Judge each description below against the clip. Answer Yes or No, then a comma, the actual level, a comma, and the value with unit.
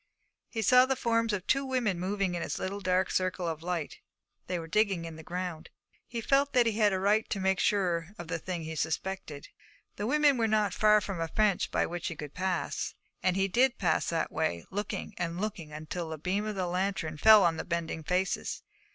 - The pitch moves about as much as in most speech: Yes, average, 4.0 semitones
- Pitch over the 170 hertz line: Yes, medium, 185 Hz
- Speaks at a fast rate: Yes, fast, 220 wpm